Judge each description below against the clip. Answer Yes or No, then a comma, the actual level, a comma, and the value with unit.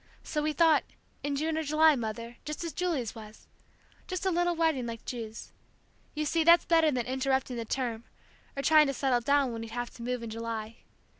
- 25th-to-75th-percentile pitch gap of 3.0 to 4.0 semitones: No, average, 5.2 semitones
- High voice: Yes, very high, 270 Hz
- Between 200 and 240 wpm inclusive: Yes, fast, 205 wpm